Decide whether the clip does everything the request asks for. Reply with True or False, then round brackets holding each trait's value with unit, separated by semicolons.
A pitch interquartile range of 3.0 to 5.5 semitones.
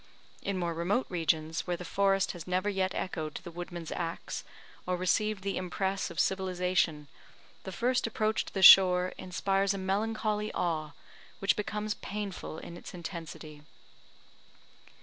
False (2.5 semitones)